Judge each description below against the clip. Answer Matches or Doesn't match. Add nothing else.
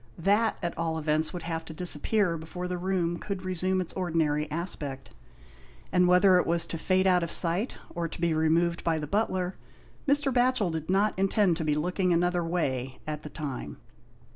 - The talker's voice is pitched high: Doesn't match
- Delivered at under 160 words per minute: Doesn't match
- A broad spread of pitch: Doesn't match